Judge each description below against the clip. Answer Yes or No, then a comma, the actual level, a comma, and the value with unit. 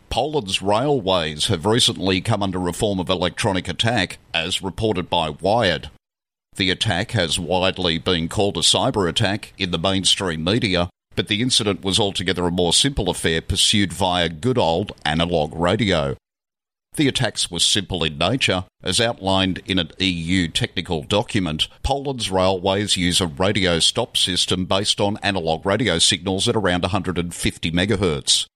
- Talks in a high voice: No, very low, 95 Hz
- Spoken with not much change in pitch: No, average, 3.0 semitones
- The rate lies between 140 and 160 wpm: Yes, average, 150 wpm